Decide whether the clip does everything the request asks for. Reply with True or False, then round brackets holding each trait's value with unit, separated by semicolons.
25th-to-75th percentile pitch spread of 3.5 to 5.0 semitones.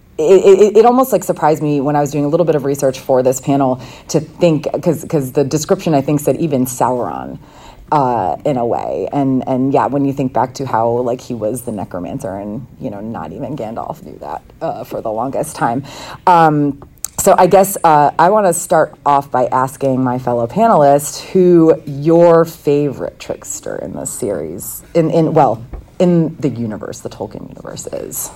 True (4.2 semitones)